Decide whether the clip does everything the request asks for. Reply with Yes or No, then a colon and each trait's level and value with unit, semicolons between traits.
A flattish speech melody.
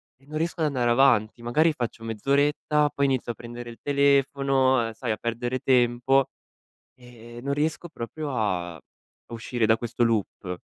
No: average, 3.1 semitones